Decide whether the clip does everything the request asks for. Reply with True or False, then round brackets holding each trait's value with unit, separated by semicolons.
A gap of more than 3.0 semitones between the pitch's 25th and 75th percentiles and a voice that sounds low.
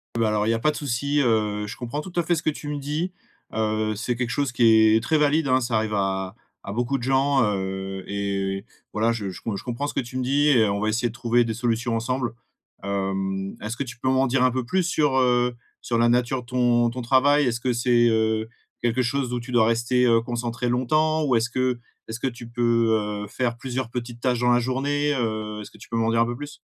False (2.7 semitones; 120 Hz)